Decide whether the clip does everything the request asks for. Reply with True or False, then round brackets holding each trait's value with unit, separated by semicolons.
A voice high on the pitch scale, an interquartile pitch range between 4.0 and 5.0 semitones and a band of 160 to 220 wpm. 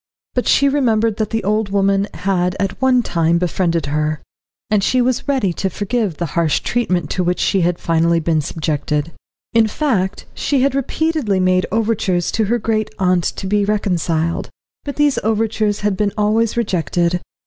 True (200 Hz; 4.5 semitones; 170 wpm)